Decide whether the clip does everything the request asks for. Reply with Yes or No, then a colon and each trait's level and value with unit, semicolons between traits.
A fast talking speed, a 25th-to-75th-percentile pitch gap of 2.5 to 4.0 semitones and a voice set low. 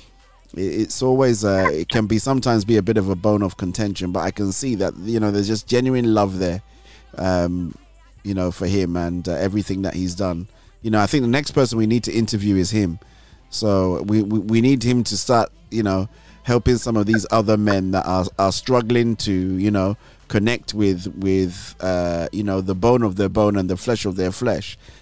Yes: fast, 220 wpm; average, 3.1 semitones; low, 105 Hz